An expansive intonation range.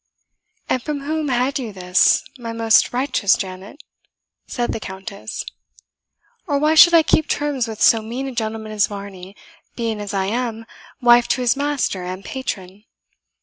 No: average, 5.0 semitones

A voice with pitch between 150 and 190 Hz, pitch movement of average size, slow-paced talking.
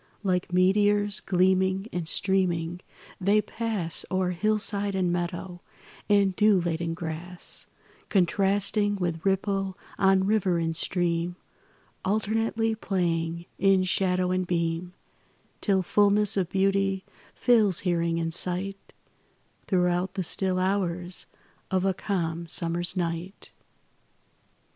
No: medium, 185 Hz; narrow, 2.1 semitones; slow, 110 wpm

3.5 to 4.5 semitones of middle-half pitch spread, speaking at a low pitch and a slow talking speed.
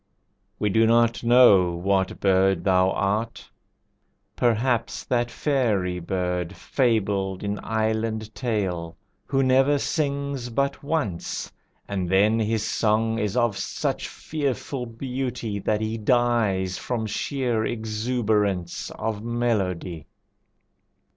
Yes: average, 3.9 semitones; low, 110 Hz; slow, 110 wpm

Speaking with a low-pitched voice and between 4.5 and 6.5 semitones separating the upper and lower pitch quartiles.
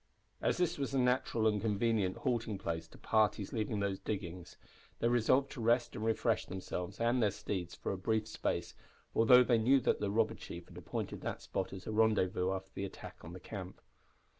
No: low, 110 Hz; average, 3.6 semitones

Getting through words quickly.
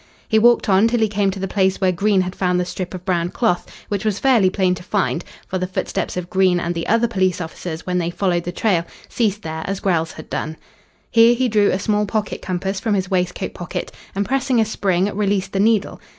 Yes: fast, 235 wpm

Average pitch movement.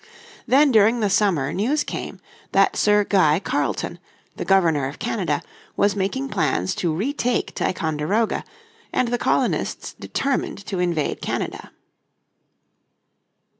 No: wide, 6.1 semitones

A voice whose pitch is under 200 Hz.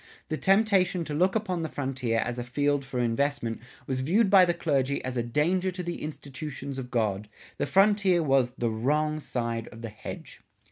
Yes: medium, 140 Hz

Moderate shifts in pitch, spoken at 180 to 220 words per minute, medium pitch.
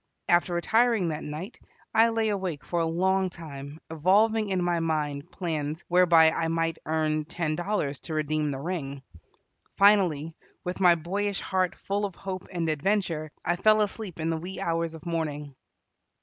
No: average, 3.6 semitones; average, 165 wpm; medium, 170 Hz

